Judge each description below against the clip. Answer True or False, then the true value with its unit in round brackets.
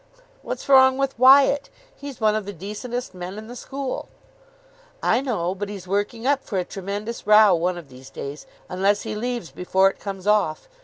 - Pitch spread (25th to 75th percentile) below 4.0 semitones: False (4.8 semitones)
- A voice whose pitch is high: True (210 Hz)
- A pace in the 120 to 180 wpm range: False (190 wpm)